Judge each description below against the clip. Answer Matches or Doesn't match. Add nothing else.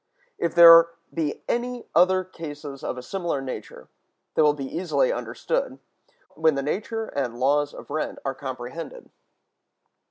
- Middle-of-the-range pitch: Matches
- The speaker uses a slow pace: Doesn't match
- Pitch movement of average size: Matches